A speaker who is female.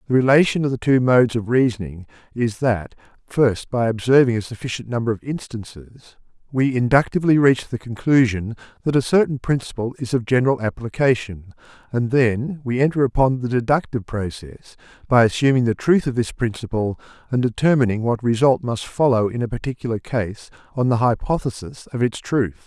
No: male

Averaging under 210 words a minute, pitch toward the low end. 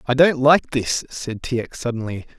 Yes: average, 200 wpm; low, 130 Hz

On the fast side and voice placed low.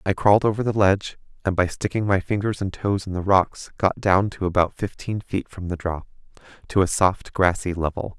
Yes: fast, 215 wpm; very low, 95 Hz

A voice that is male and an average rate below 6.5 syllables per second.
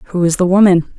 No: female; 5.4 syllables/s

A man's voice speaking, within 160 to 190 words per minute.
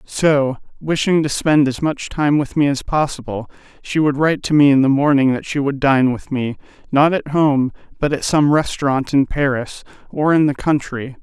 No: male; fast, 205 wpm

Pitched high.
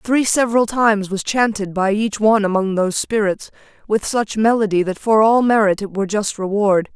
Yes: high, 210 Hz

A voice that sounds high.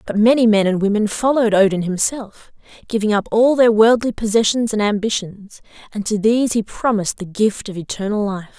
Yes: high, 215 Hz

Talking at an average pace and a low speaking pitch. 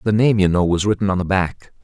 No: fast, 295 wpm; very low, 95 Hz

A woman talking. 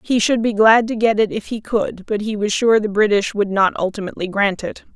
Yes: female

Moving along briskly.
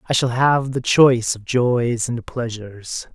No: average, 170 wpm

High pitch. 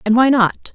Yes: high, 235 Hz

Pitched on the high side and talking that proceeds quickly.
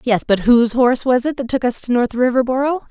Yes: high, 245 Hz; fast, 250 wpm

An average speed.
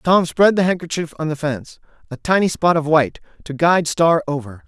Yes: average, 195 wpm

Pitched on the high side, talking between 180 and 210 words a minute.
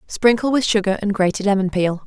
Yes: high, 205 Hz; fast, 205 wpm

